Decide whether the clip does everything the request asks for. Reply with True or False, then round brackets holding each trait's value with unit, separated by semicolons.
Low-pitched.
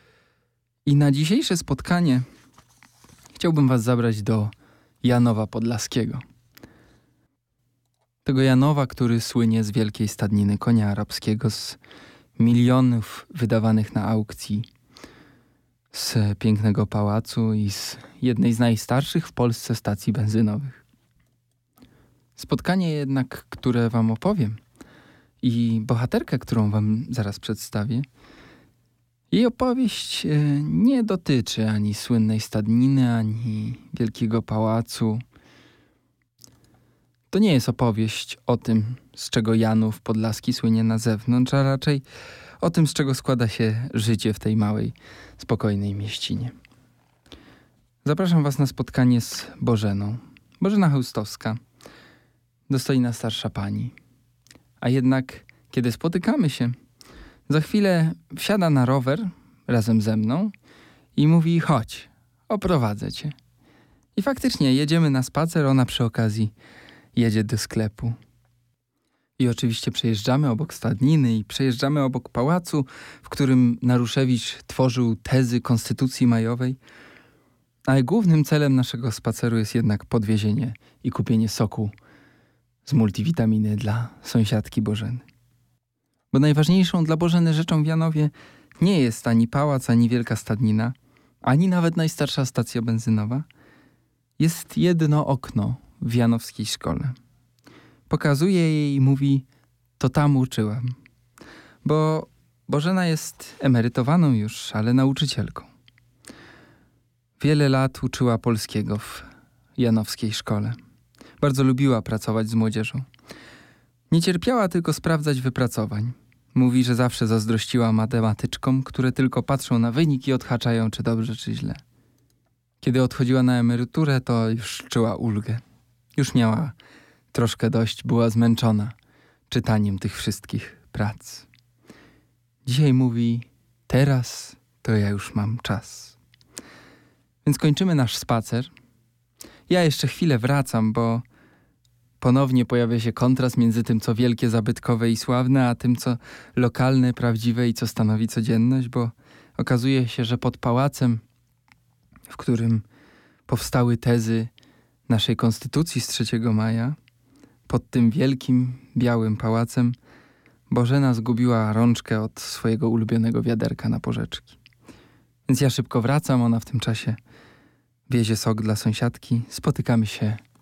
True (120 Hz)